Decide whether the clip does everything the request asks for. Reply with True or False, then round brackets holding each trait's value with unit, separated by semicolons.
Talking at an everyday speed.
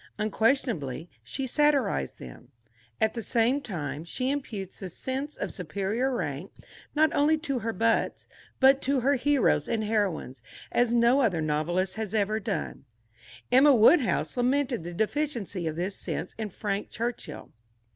True (145 wpm)